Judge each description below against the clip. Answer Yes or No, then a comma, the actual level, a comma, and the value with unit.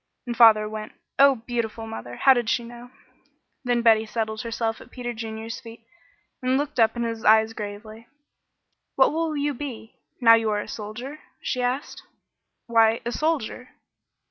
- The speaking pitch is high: Yes, high, 230 Hz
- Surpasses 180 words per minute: No, average, 165 wpm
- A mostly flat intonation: Yes, narrow, 2.1 semitones